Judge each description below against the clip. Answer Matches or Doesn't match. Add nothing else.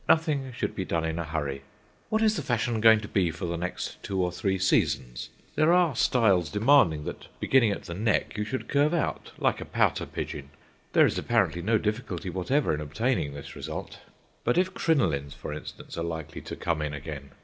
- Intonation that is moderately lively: Doesn't match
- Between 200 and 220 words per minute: Matches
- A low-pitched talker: Matches